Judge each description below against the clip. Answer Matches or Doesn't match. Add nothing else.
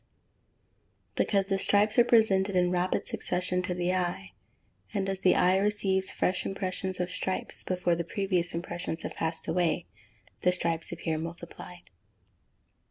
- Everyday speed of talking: Matches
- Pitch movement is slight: Matches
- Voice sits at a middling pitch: Matches